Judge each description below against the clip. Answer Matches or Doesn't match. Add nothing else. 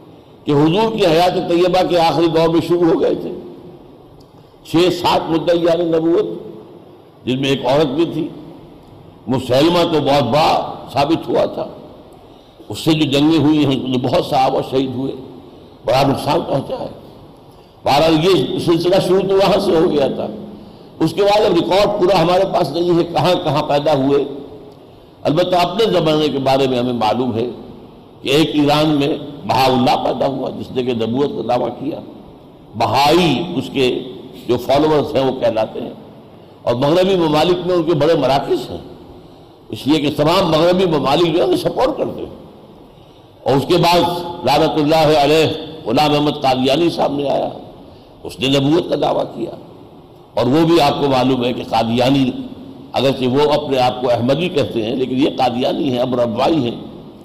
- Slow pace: Doesn't match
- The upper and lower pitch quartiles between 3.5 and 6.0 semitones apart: Matches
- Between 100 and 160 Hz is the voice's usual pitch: Matches